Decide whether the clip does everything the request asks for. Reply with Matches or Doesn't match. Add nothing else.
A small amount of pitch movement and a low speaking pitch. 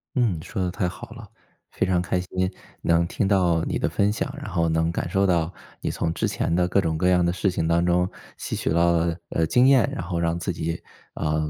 Matches